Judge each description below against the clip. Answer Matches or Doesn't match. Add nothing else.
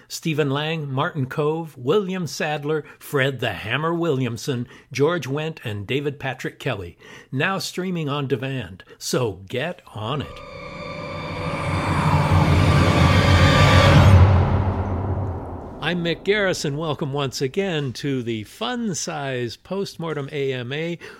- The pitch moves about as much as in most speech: Matches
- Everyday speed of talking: Doesn't match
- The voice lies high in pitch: Doesn't match